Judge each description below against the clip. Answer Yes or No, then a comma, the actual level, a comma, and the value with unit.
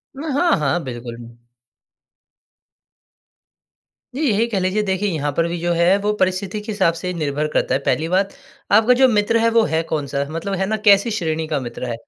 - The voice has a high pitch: No, medium, 180 Hz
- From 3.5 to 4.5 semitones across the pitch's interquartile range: No, average, 5.2 semitones